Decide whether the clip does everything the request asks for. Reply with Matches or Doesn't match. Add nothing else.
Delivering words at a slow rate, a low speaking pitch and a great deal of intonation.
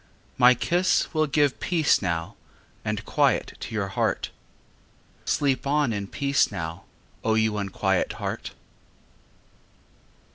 Matches